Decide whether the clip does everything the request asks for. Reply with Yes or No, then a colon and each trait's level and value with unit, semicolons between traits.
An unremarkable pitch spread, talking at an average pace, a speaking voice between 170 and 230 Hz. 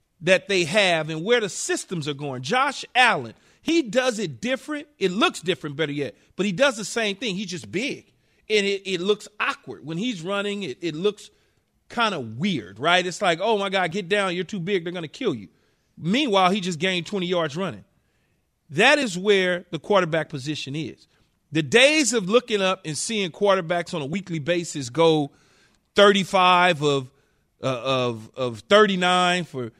Yes: average, 4.4 semitones; average, 185 wpm; medium, 185 Hz